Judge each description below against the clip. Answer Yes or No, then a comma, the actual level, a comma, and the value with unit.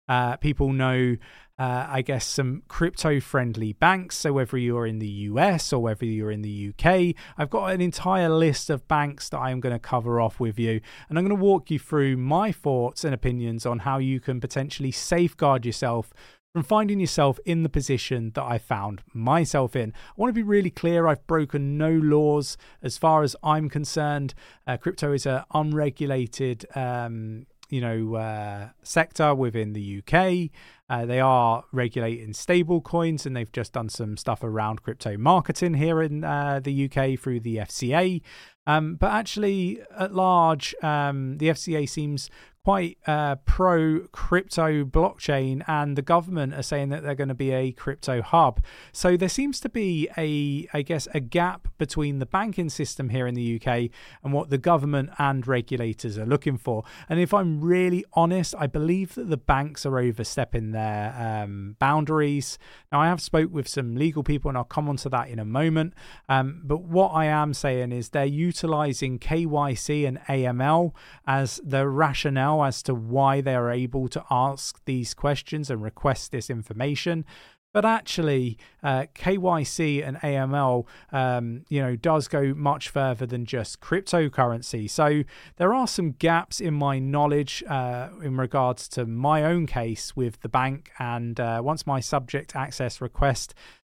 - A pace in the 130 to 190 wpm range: Yes, average, 175 wpm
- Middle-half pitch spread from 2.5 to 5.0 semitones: Yes, average, 4.2 semitones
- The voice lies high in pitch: No, medium, 140 Hz